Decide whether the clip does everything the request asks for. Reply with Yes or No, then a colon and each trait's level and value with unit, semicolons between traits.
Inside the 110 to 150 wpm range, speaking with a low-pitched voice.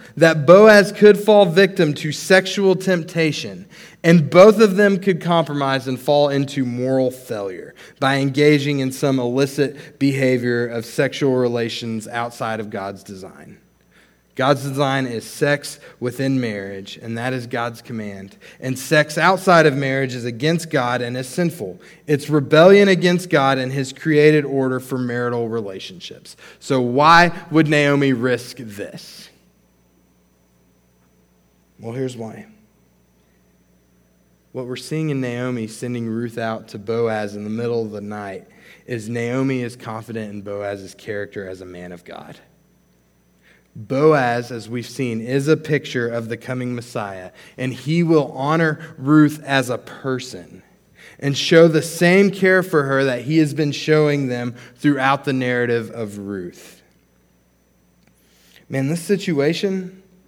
Yes: average, 140 wpm; low, 130 Hz